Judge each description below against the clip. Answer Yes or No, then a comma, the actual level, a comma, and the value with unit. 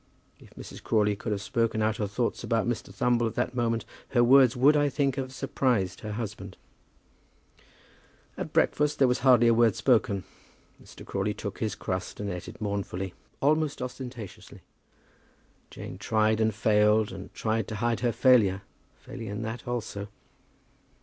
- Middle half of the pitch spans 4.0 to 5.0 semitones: No, average, 3.0 semitones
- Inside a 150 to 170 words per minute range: Yes, average, 165 wpm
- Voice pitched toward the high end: No, low, 115 Hz